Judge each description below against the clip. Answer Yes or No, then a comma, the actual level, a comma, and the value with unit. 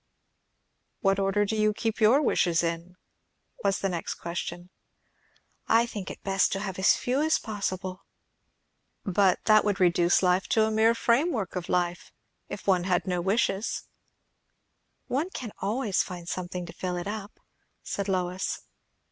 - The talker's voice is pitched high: Yes, high, 195 Hz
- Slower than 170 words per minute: Yes, average, 155 wpm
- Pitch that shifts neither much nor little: Yes, average, 3.2 semitones